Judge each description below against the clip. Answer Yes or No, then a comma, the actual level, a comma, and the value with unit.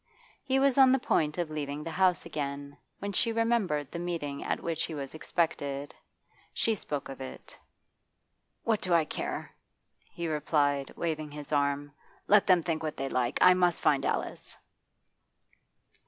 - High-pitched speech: No, medium, 155 Hz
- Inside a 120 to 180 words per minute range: Yes, average, 160 wpm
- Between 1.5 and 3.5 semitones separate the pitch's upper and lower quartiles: No, average, 4.2 semitones